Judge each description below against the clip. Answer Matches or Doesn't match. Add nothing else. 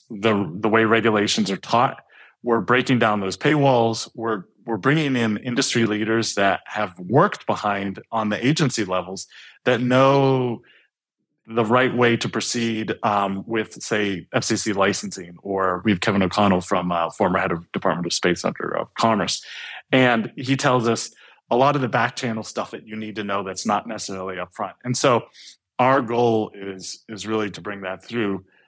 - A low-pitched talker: Matches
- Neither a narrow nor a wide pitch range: Matches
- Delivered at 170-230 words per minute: Matches